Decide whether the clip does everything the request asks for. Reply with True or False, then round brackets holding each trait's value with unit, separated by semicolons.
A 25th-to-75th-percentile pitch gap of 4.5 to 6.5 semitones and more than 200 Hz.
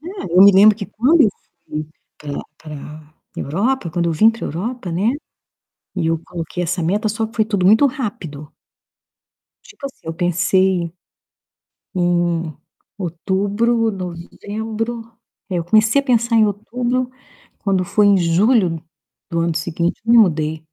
False (5.0 semitones; 190 Hz)